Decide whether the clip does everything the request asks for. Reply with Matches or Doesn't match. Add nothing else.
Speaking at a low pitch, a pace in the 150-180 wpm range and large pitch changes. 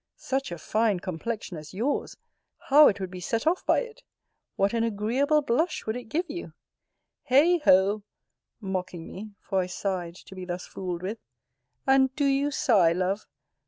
Doesn't match